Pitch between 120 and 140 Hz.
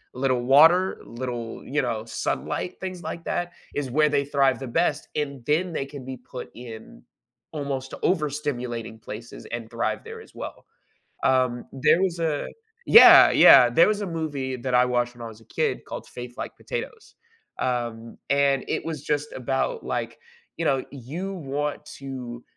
Yes: low, 135 Hz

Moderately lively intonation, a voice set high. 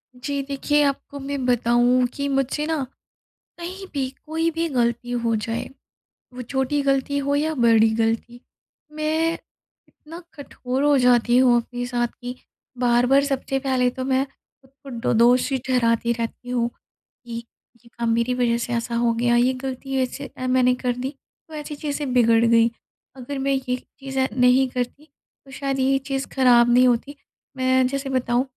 No: narrow, 2.3 semitones; very high, 255 Hz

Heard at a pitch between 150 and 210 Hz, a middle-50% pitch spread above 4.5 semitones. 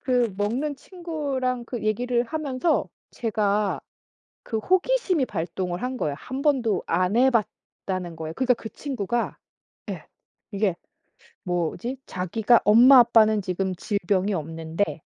No: high, 220 Hz; wide, 5.4 semitones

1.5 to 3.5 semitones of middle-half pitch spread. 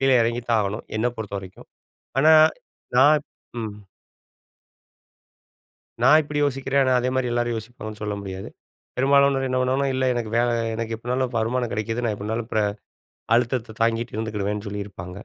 Yes: average, 3.2 semitones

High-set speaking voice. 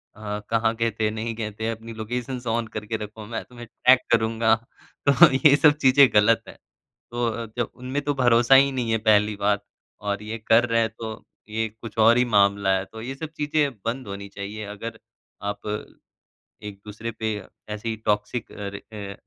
No: low, 115 Hz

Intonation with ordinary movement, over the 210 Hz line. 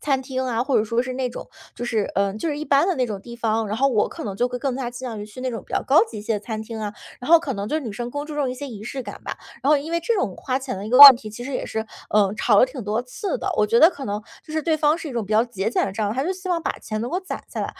Yes: average, 4.8 semitones; very high, 250 Hz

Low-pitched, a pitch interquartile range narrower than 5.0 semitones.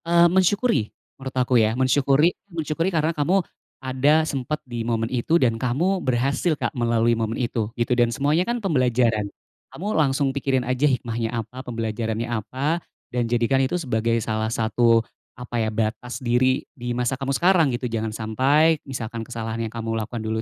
Yes: low, 125 Hz; average, 4.1 semitones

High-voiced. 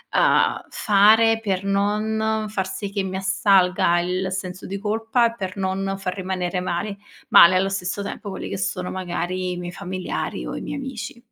Yes: high, 195 Hz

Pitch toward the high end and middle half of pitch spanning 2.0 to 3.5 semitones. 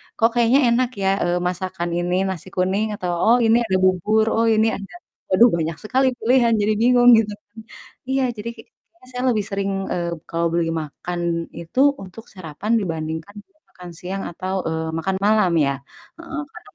No: high, 200 Hz; average, 4.8 semitones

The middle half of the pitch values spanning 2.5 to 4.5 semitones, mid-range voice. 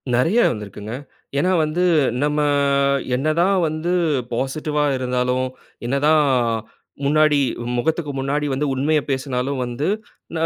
Yes: average, 3.3 semitones; medium, 145 Hz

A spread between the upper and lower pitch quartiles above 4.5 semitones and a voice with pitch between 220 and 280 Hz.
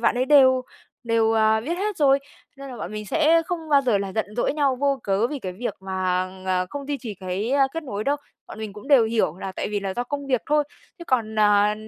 Yes: average, 5.3 semitones; high, 235 Hz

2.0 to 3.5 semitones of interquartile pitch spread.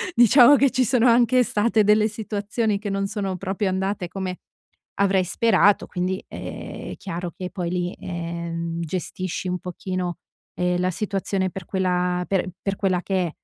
Yes: narrow, 2.6 semitones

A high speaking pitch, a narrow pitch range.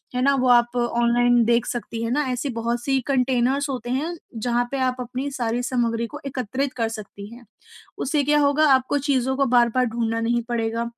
Yes: high, 245 Hz; narrow, 2.2 semitones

